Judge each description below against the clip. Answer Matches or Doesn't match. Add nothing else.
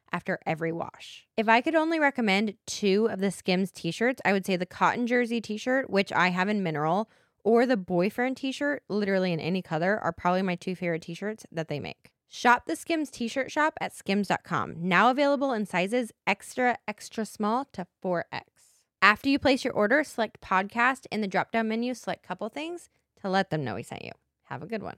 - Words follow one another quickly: Matches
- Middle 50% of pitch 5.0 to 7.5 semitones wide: Matches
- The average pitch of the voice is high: Matches